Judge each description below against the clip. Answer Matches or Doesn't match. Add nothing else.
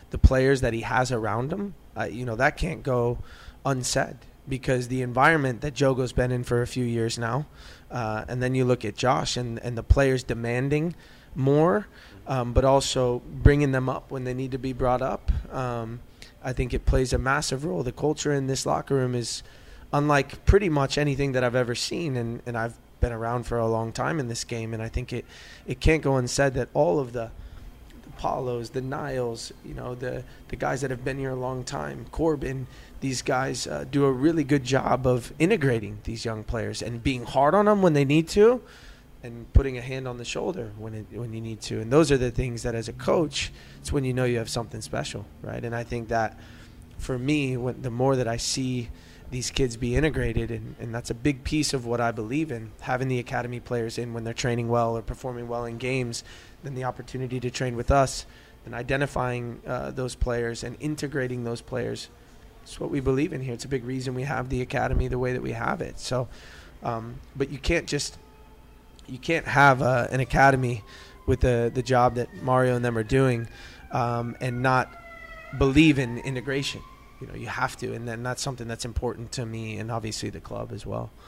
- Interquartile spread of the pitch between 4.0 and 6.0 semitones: Doesn't match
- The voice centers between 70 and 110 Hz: Doesn't match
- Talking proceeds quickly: Matches